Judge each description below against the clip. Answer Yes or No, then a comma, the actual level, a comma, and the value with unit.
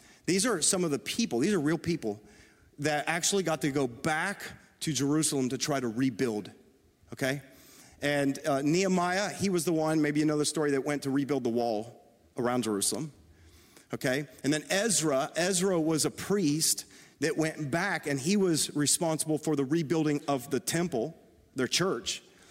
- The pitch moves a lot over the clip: No, average, 3.8 semitones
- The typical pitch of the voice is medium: Yes, medium, 150 Hz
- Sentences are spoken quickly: No, average, 175 wpm